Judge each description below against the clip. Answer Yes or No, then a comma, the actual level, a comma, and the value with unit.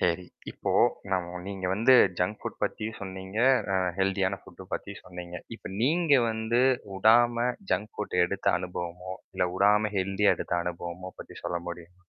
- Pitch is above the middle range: No, very low, 95 Hz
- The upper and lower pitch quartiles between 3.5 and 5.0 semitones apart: No, average, 3.1 semitones